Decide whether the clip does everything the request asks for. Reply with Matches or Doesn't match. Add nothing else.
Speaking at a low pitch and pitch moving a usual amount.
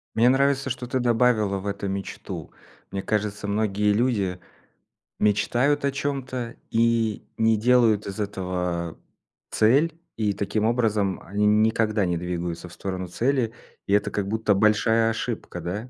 Matches